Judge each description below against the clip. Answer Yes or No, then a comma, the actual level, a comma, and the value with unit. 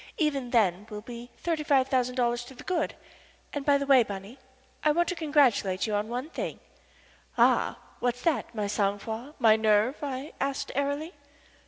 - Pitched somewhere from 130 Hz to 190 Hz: No, very high, 250 Hz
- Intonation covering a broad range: No, average, 4.6 semitones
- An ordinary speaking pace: Yes, average, 180 wpm